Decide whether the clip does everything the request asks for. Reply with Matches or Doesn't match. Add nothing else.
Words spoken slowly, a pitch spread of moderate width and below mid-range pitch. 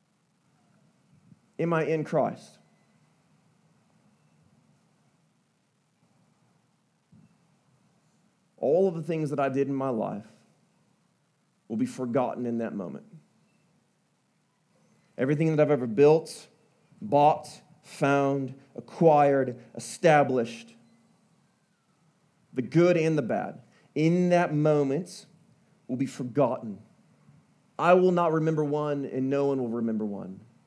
Doesn't match